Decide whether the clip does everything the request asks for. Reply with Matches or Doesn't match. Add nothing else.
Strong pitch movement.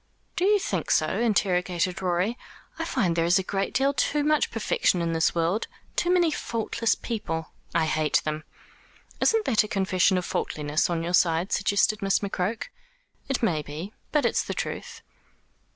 Matches